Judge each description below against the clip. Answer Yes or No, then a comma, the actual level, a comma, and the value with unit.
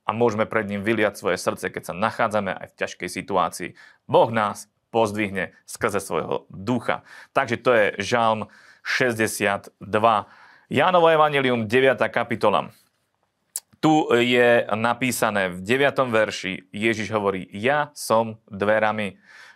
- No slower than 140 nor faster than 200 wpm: No, average, 125 wpm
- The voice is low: Yes, low, 110 Hz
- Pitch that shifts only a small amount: No, average, 3.3 semitones